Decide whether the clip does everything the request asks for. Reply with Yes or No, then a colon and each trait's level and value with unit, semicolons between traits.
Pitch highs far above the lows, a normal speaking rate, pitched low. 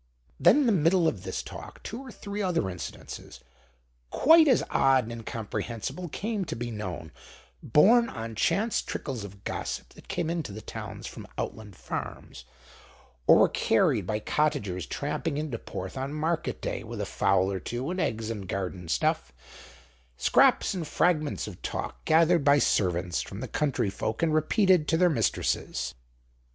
Yes: wide, 8.5 semitones; average, 165 wpm; low, 130 Hz